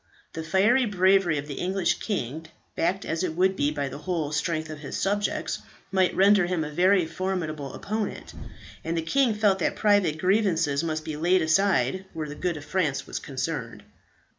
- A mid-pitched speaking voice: Yes, medium, 170 Hz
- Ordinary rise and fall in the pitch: Yes, average, 3.8 semitones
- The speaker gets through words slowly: No, average, 185 wpm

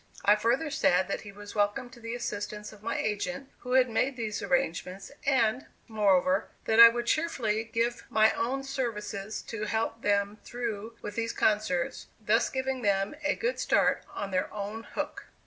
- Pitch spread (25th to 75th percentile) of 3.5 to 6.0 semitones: No, average, 3.0 semitones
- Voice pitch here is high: Yes, high, 220 Hz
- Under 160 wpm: No, average, 175 wpm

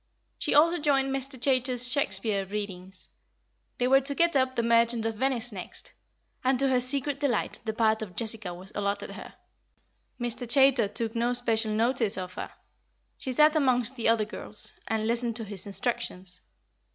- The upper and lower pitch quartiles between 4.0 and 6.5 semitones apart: No, average, 3.6 semitones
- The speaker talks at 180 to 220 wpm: No, average, 170 wpm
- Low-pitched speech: No, high, 235 Hz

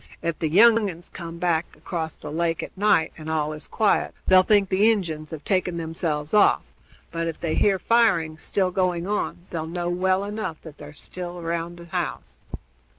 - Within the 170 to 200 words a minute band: Yes, average, 190 wpm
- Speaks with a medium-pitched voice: Yes, medium, 170 Hz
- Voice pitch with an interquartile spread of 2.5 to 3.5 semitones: Yes, average, 2.8 semitones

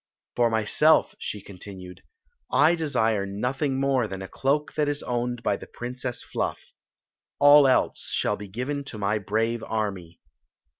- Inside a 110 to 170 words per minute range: Yes, average, 150 wpm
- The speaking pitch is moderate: No, low, 120 Hz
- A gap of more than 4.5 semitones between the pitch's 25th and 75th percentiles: Yes, average, 5.0 semitones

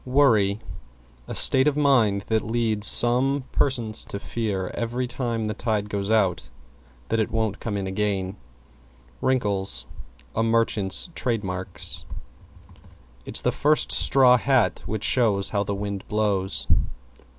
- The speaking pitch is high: No, low, 110 Hz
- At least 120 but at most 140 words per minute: Yes, slow, 135 wpm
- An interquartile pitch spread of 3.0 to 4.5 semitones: Yes, average, 3.4 semitones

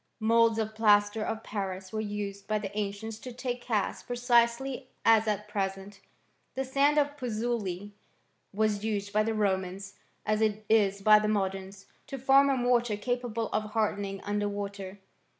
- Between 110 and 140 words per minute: No, average, 160 wpm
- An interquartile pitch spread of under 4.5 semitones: Yes, narrow, 2.5 semitones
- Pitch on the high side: Yes, high, 215 Hz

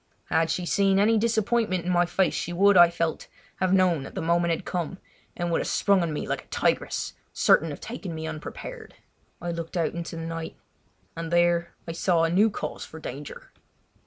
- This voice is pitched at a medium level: Yes, medium, 175 Hz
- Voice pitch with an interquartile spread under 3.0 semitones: Yes, narrow, 2.5 semitones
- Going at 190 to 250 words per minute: Yes, average, 200 wpm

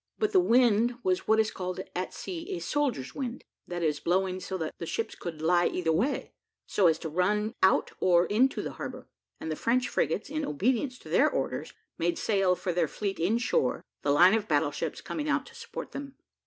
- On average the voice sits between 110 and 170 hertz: No, high, 190 Hz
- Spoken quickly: Yes, fast, 210 wpm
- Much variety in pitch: Yes, wide, 6.2 semitones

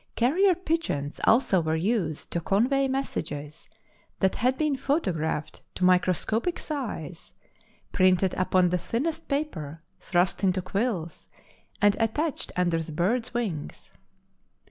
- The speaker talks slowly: Yes, slow, 120 wpm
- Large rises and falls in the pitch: Yes, wide, 7.5 semitones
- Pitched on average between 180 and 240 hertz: Yes, high, 190 Hz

